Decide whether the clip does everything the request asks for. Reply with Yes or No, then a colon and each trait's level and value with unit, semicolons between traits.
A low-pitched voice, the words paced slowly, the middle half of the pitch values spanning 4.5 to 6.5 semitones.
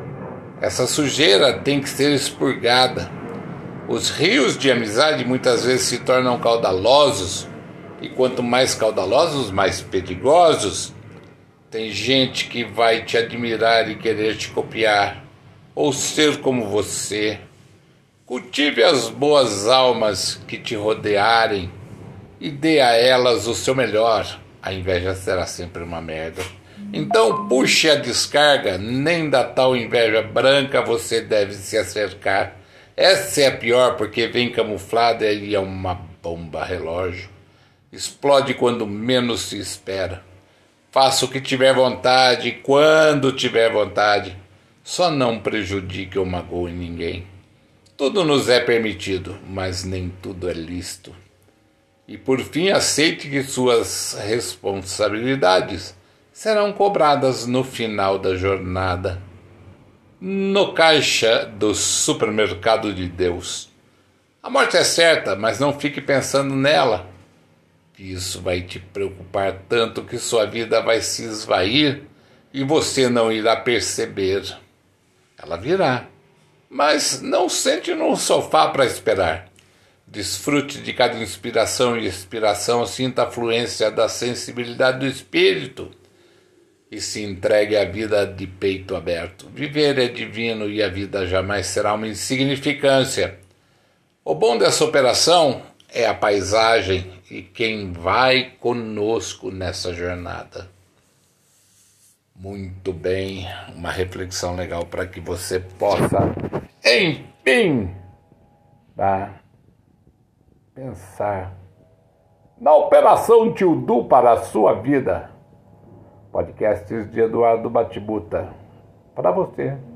Yes: low, 110 Hz; slow, 115 wpm; average, 5.2 semitones